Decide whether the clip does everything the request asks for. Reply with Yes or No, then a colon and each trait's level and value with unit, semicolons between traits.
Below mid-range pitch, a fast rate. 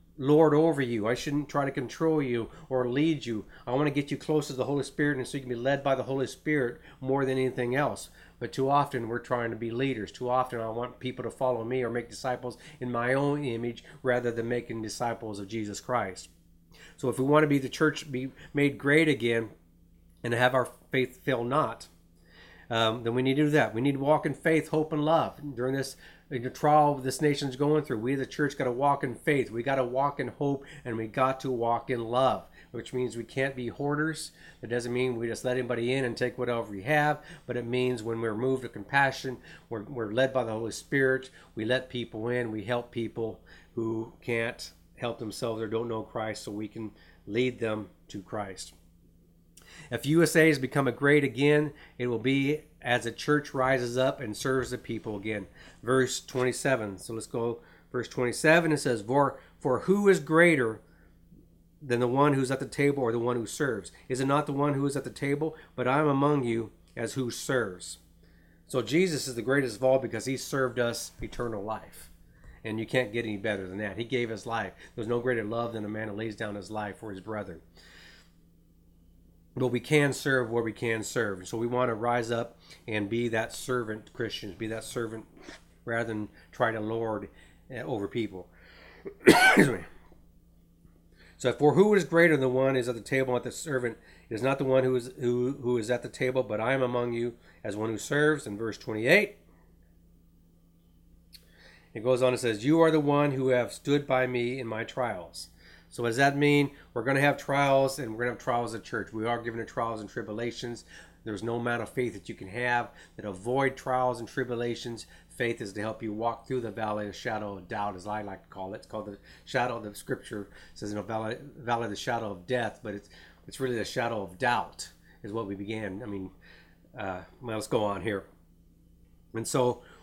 Yes: low, 120 Hz; fast, 220 wpm